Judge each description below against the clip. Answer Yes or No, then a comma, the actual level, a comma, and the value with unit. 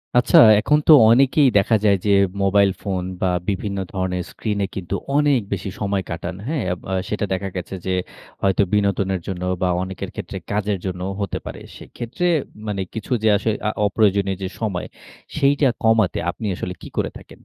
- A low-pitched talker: Yes, low, 100 Hz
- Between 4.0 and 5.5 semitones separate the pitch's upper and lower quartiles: No, average, 2.8 semitones